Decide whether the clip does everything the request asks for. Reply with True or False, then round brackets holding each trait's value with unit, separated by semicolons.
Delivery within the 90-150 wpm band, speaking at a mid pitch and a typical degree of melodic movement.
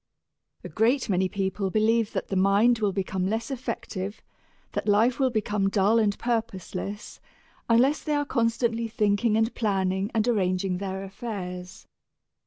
False (145 wpm; 210 Hz; 3.1 semitones)